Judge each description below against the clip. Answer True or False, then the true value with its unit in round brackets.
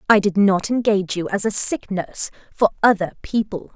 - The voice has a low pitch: False (200 Hz)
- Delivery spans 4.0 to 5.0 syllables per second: False (5.4 syllables/s)